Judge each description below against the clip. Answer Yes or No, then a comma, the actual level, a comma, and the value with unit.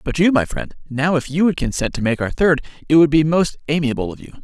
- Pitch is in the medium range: Yes, medium, 150 Hz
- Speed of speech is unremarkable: No, fast, 255 wpm